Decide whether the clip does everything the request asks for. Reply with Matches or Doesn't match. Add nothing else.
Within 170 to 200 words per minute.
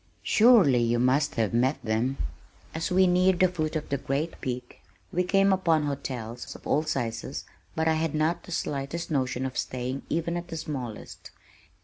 Matches